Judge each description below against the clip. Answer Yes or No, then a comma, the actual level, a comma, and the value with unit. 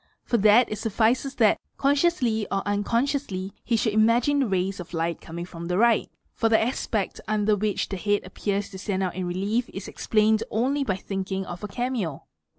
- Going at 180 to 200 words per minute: Yes, average, 190 wpm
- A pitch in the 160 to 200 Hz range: No, high, 210 Hz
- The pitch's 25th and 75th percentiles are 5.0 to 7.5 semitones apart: No, average, 3.6 semitones